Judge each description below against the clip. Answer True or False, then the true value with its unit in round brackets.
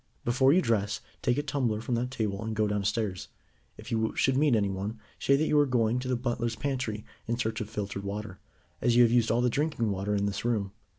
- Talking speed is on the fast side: True (230 wpm)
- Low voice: True (115 Hz)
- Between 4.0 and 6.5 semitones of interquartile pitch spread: False (3.3 semitones)